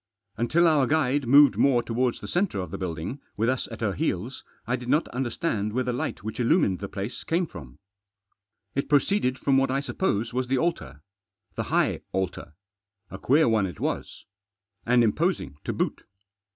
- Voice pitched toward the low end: Yes, low, 125 Hz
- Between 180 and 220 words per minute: Yes, average, 185 wpm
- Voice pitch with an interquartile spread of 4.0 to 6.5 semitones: Yes, average, 5.3 semitones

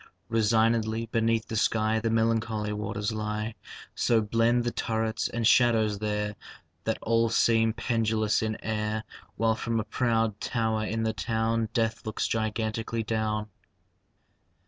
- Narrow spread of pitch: Yes, narrow, 0.9 semitones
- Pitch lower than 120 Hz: Yes, low, 110 Hz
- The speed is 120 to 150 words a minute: Yes, slow, 135 wpm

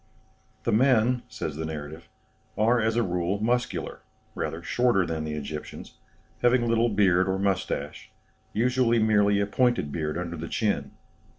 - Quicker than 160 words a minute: No, average, 150 wpm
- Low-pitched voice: Yes, low, 100 Hz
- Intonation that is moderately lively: No, wide, 6.0 semitones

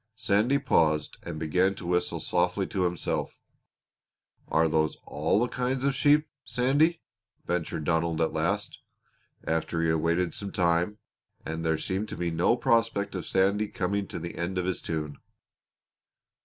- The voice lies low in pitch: Yes, very low, 90 Hz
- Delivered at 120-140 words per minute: No, average, 165 wpm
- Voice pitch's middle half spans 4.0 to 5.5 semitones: Yes, average, 4.5 semitones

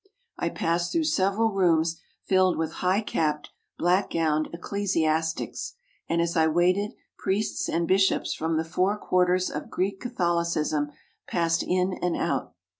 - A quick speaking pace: No, average, 140 wpm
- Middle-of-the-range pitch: Yes, medium, 175 Hz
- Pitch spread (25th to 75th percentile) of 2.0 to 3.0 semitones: Yes, average, 2.7 semitones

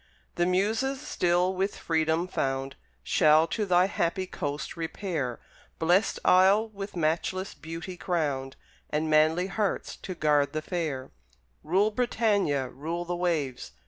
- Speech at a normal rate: No, slow, 130 wpm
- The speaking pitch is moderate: Yes, medium, 175 Hz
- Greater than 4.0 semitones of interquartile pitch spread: No, average, 3.6 semitones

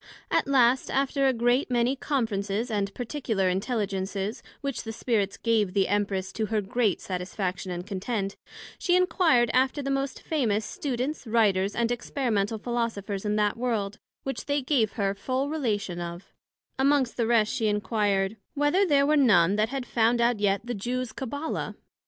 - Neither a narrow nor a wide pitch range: Yes, average, 4.4 semitones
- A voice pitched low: No, high, 230 Hz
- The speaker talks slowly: No, average, 165 wpm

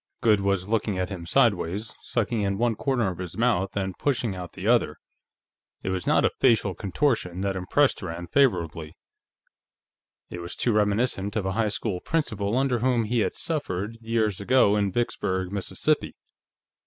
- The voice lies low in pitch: Yes, low, 100 Hz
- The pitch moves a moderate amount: Yes, average, 4.0 semitones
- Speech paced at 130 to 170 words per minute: Yes, average, 165 wpm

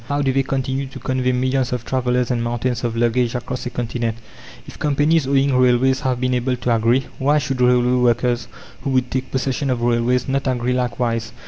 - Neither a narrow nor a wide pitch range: No, narrow, 1.5 semitones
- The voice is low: Yes, low, 125 Hz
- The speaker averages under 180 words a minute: No, average, 200 wpm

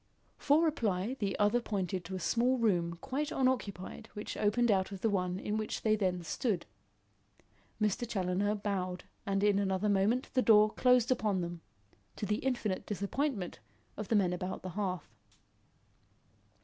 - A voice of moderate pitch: No, high, 205 Hz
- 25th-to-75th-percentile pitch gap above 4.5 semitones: No, average, 3.6 semitones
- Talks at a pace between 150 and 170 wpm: Yes, average, 160 wpm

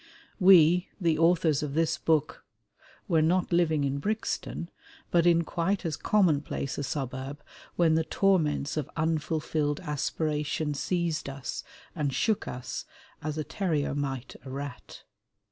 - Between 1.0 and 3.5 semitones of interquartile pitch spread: Yes, average, 3.0 semitones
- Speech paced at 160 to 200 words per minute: No, slow, 135 wpm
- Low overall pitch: No, medium, 155 Hz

